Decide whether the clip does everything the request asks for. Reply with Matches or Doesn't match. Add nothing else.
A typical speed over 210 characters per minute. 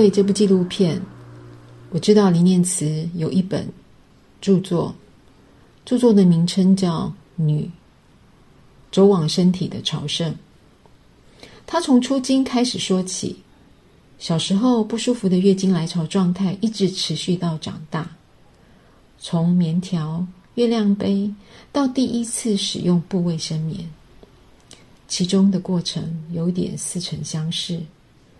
Doesn't match